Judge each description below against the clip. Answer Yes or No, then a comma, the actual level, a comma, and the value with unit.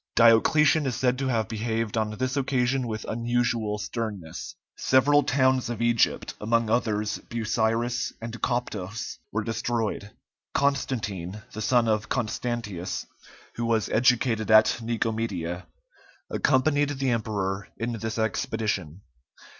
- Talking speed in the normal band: No, slow, 120 wpm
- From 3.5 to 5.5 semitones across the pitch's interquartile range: No, narrow, 2.4 semitones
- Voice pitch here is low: Yes, low, 115 Hz